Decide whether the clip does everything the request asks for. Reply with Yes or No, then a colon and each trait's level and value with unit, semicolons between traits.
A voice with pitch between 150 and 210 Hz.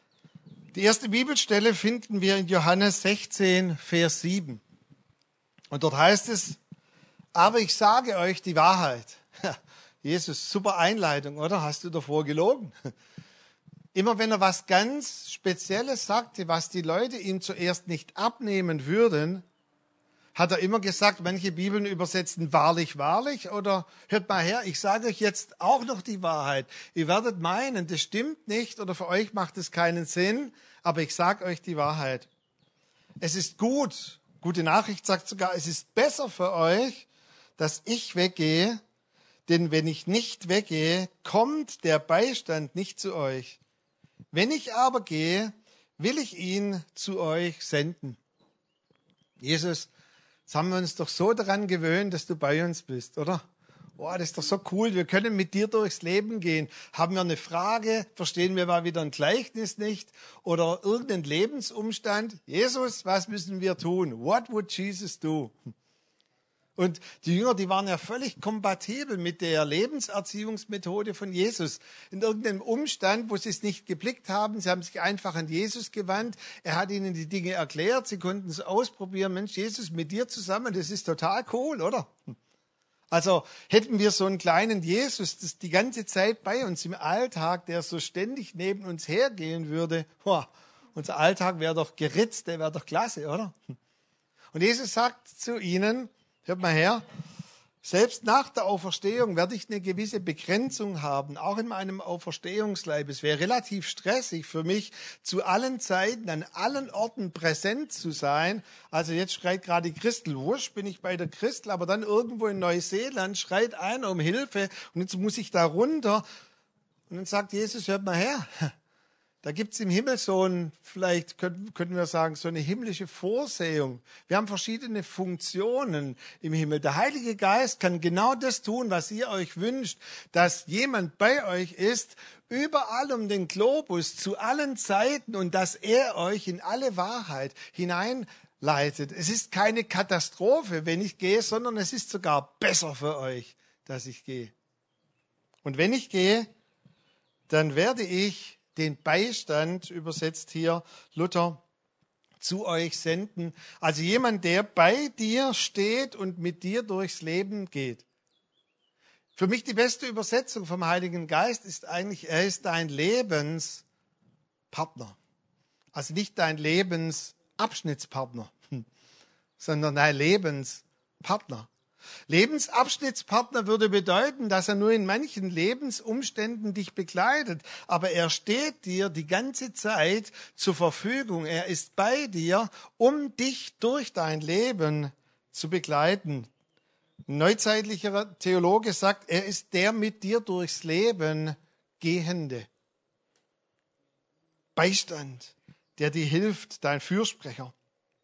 Yes: medium, 185 Hz